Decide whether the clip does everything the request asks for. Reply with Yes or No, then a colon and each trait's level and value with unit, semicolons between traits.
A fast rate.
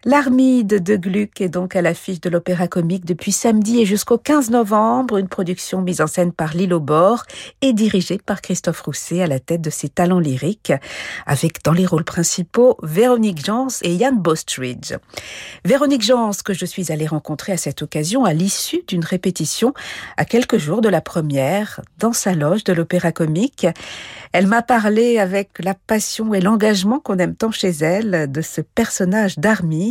No: average, 180 wpm